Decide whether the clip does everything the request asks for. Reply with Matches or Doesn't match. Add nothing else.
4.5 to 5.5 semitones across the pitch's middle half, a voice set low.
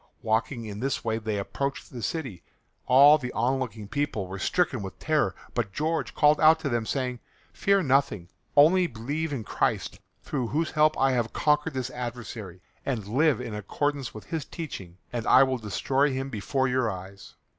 Matches